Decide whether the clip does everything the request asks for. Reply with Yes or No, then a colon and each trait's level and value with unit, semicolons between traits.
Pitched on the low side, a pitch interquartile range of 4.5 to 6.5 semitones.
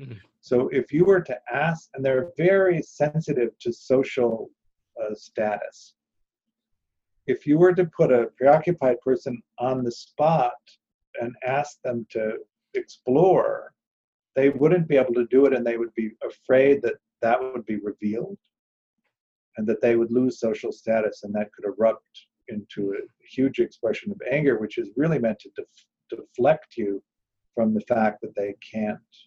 Yes: low, 130 Hz; average, 5.1 semitones